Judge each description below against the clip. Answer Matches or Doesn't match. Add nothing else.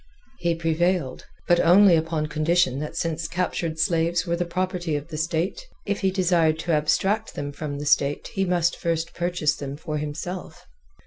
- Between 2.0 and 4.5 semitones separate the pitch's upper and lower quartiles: Matches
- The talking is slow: Doesn't match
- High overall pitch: Doesn't match